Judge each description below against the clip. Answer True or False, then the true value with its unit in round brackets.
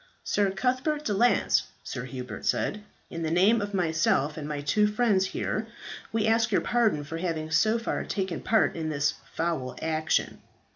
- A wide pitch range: True (5.7 semitones)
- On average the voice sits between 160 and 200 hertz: True (185 Hz)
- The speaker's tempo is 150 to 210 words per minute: True (175 wpm)